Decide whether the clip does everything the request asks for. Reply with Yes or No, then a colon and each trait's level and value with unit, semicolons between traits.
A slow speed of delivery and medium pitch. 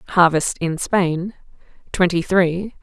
Yes: slow, 105 wpm; medium, 175 Hz